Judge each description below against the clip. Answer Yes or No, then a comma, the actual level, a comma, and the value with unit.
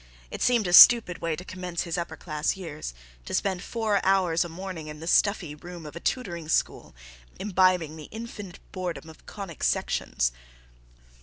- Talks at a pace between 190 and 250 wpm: No, average, 170 wpm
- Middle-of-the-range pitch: Yes, medium, 175 Hz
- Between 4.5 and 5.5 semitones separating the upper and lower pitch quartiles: No, average, 3.2 semitones